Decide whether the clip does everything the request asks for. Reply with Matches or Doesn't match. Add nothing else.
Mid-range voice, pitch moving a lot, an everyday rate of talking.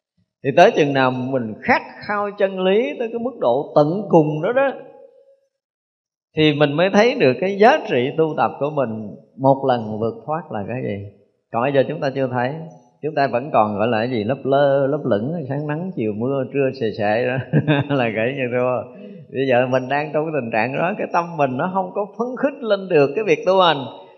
Matches